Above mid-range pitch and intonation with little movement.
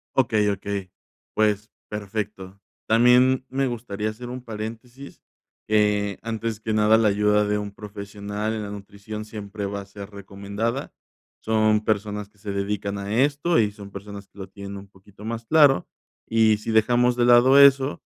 No: low, 105 Hz; narrow, 2.1 semitones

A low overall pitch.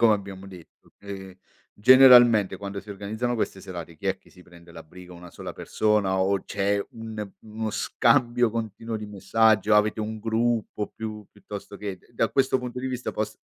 Yes: low, 105 Hz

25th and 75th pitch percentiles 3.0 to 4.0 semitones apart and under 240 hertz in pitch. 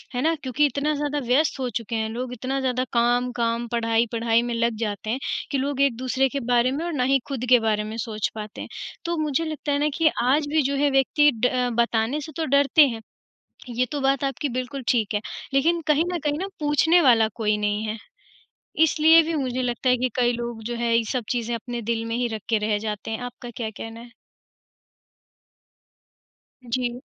No: average, 3.5 semitones; very high, 250 Hz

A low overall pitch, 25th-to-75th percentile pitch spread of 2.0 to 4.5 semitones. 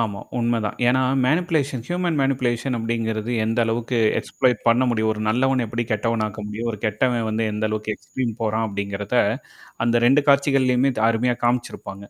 Yes: low, 115 Hz; average, 2.9 semitones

